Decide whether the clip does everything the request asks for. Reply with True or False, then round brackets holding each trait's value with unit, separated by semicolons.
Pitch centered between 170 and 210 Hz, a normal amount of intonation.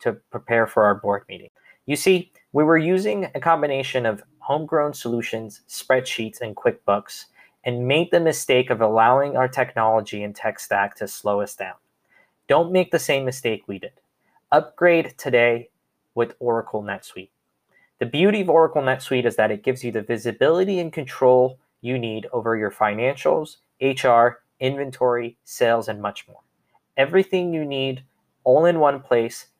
False (130 Hz; 4.7 semitones)